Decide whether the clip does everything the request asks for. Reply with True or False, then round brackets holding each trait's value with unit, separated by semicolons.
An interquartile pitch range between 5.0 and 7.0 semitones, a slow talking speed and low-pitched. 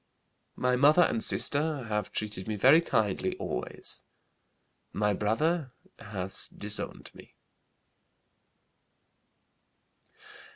True (5.6 semitones; 85 wpm; 110 Hz)